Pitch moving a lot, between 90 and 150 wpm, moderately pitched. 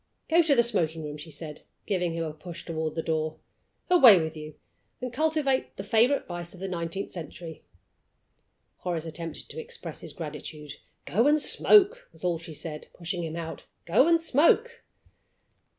No: wide, 8.9 semitones; average, 170 wpm; medium, 175 Hz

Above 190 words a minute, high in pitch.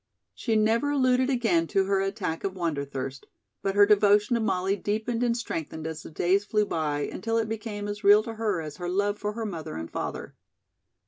Yes: average, 200 wpm; high, 205 Hz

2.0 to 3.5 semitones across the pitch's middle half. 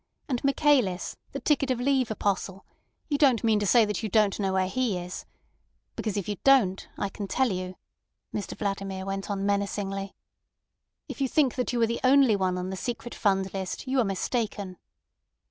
No: average, 4.5 semitones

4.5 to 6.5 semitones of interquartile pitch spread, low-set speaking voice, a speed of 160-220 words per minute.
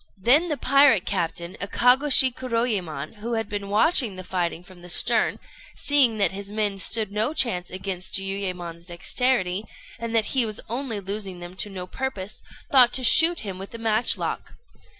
No: average, 4.8 semitones; high, 210 Hz; average, 170 wpm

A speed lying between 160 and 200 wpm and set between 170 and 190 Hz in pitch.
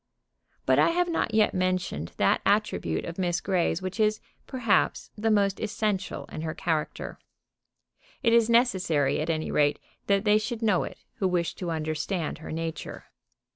Yes: average, 165 wpm; medium, 185 Hz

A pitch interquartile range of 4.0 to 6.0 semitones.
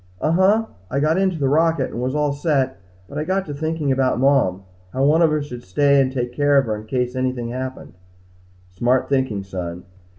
No: average, 3.5 semitones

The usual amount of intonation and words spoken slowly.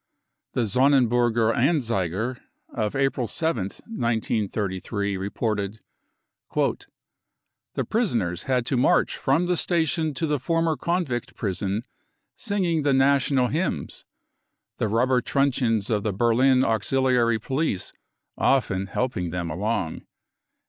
Yes: average, 5.0 semitones; slow, 110 wpm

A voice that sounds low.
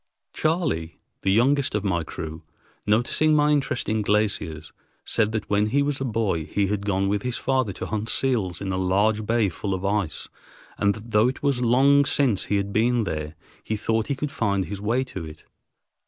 Yes: low, 105 Hz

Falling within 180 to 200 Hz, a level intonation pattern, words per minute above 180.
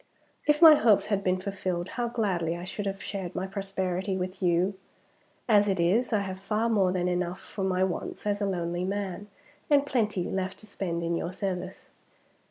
Yes: high, 190 Hz; narrow, 2.2 semitones; average, 190 wpm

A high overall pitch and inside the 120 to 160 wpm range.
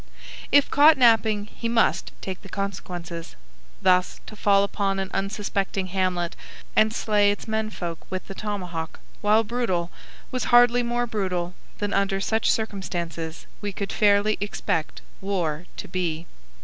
Yes: high, 200 Hz; average, 145 wpm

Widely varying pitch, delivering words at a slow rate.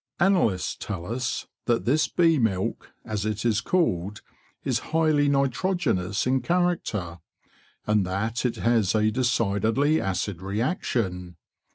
Yes: wide, 6.3 semitones; slow, 125 wpm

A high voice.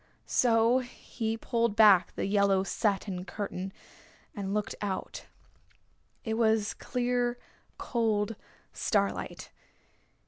Yes: high, 215 Hz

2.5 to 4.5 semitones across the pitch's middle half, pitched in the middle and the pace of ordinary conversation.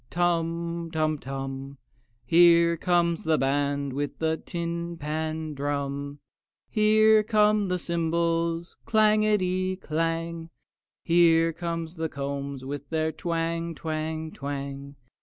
No: average, 2.9 semitones; medium, 165 Hz; slow, 105 wpm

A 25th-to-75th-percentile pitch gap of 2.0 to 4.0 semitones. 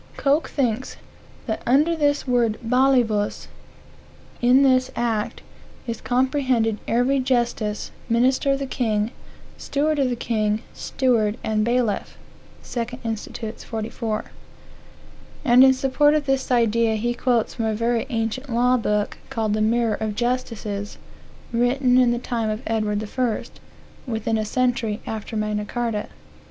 Yes: average, 2.8 semitones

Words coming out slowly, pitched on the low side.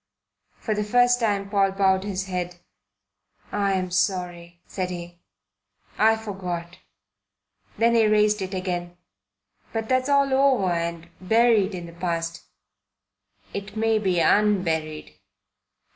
No: slow, 120 wpm; high, 195 Hz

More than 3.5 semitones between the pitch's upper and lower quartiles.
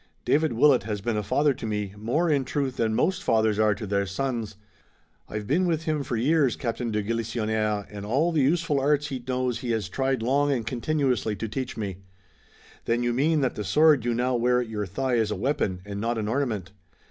Yes: average, 4.4 semitones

